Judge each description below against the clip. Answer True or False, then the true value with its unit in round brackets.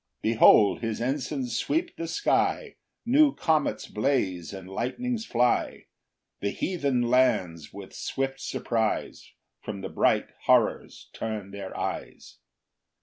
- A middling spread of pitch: False (6.1 semitones)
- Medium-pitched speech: False (120 Hz)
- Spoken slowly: True (120 wpm)